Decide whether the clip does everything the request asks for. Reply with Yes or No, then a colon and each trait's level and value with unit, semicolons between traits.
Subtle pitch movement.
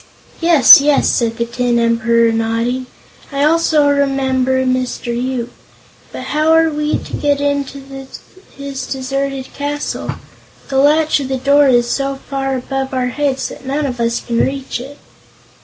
Yes: narrow, 2.3 semitones